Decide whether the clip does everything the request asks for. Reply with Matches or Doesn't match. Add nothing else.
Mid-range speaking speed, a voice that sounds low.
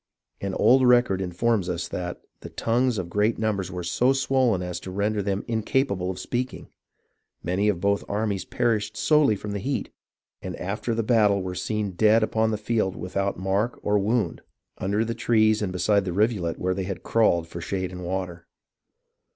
Matches